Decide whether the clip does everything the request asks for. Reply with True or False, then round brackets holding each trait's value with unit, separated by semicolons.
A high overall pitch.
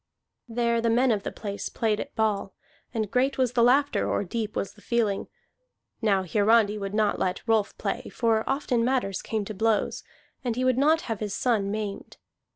True (220 Hz)